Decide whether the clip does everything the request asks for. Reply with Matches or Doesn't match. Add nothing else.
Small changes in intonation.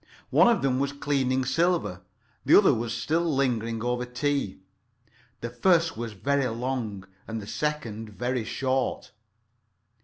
Doesn't match